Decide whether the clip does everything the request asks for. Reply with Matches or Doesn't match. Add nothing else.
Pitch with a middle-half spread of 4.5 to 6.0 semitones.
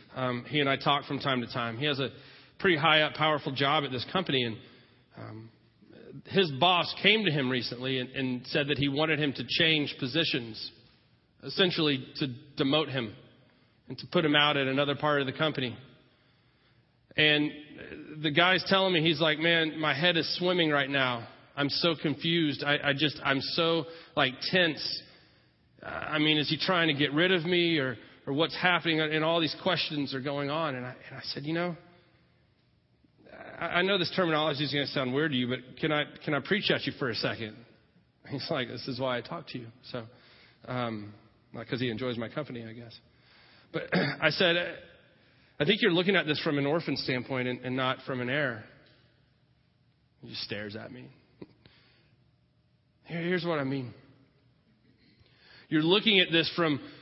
Doesn't match